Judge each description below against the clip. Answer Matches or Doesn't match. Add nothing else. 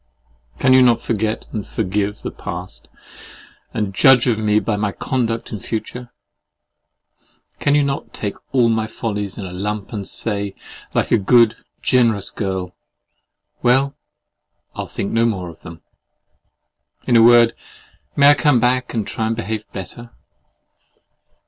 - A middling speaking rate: Matches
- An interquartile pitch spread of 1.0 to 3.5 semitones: Matches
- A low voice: Matches